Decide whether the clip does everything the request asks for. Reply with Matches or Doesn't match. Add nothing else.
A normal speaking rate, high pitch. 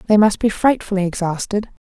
Matches